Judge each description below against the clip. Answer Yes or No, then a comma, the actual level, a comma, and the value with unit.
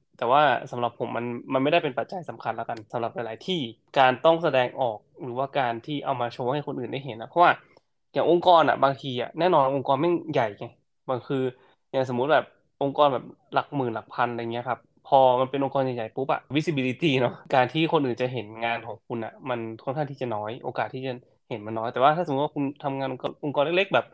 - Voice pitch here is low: Yes, low, 130 Hz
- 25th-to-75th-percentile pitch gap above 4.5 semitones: No, average, 2.8 semitones